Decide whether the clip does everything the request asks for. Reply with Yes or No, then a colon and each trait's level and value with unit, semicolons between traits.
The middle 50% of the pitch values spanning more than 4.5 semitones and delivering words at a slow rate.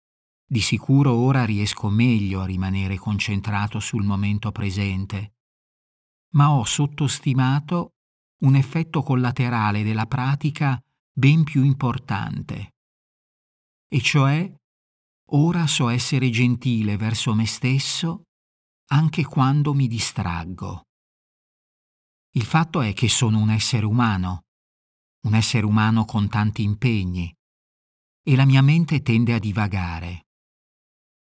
Yes: average, 5.1 semitones; slow, 105 wpm